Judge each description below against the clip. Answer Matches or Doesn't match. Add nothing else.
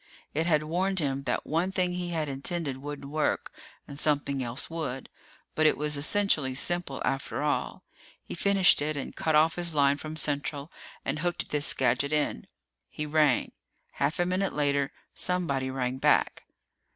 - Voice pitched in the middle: Matches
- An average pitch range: Matches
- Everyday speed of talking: Matches